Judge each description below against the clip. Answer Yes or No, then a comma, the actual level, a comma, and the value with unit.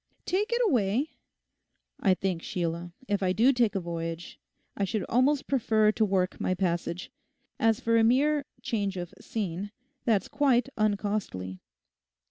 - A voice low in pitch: No, high, 205 Hz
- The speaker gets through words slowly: No, average, 145 wpm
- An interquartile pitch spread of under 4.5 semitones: No, average, 4.8 semitones